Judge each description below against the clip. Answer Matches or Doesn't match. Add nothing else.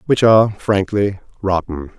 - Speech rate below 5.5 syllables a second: Matches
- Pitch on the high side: Doesn't match